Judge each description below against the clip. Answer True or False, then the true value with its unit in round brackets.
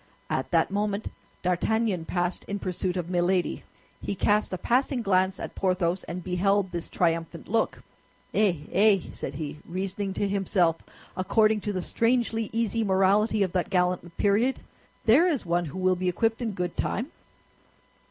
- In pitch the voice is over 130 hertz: True (190 Hz)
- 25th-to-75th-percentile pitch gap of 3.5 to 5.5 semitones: False (3.1 semitones)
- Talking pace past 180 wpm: False (160 wpm)